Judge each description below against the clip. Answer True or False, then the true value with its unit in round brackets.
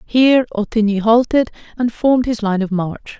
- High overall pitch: True (225 Hz)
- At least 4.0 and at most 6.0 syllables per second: True (5.1 syllables/s)